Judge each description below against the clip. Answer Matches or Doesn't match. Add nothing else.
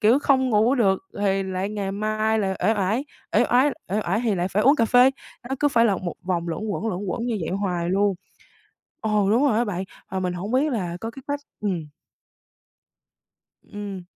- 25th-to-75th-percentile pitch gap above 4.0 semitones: Doesn't match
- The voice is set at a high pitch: Matches